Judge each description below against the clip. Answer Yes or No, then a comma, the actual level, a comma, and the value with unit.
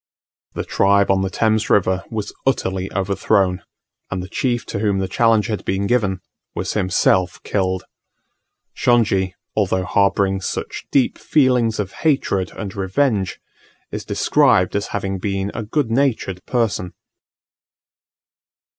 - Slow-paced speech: Yes, slow, 130 wpm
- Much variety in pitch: No, average, 3.0 semitones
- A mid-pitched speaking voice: No, low, 100 Hz